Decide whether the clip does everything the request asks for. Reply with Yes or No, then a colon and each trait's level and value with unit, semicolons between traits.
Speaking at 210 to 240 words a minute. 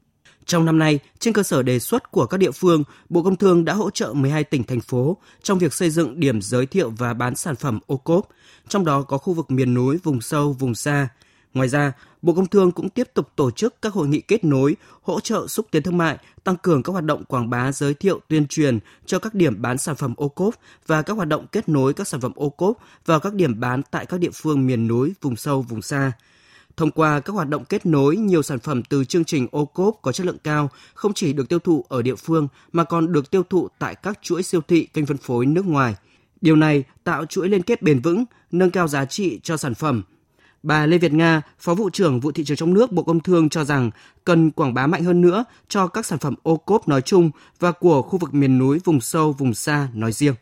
No: fast, 250 wpm